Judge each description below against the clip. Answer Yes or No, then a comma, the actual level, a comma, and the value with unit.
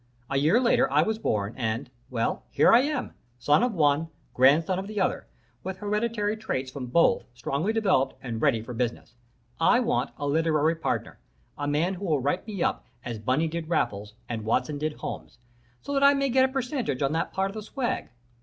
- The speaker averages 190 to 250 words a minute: Yes, average, 200 wpm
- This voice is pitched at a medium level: Yes, medium, 160 Hz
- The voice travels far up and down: Yes, wide, 8.4 semitones